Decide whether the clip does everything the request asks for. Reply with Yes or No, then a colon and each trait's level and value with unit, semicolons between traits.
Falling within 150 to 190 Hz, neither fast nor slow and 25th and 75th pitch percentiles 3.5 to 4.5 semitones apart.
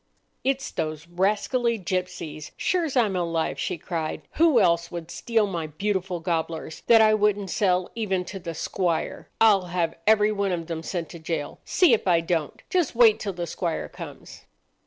Yes: medium, 185 Hz; average, 175 wpm; average, 4.2 semitones